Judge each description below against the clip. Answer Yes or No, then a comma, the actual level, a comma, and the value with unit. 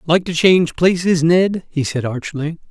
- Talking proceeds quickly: No, average, 180 wpm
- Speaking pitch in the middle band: Yes, medium, 165 Hz